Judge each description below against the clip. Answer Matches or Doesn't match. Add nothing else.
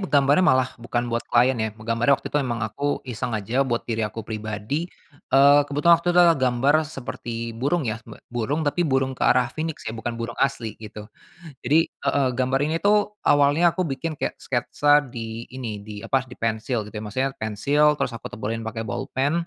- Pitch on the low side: Matches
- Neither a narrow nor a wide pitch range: Matches